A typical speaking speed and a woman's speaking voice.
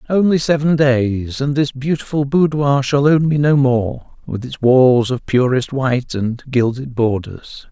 No: average, 165 wpm; male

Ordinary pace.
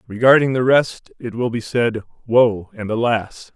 Yes: average, 170 wpm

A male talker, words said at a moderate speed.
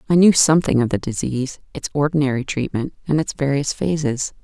No: female; average, 175 wpm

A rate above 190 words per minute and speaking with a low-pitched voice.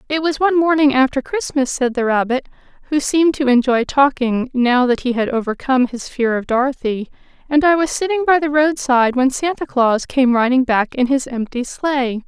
No: average, 200 wpm; very high, 265 Hz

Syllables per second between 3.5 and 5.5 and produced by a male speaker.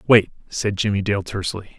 No: 5.8 syllables/s; male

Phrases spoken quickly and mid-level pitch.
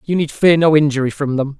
Yes: fast, 265 wpm; medium, 150 Hz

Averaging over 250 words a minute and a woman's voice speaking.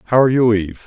No: fast, 275 wpm; male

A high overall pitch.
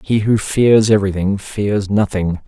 No: low, 100 Hz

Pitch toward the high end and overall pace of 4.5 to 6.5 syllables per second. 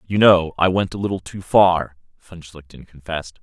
No: very low, 90 Hz; 5.0 syllables/s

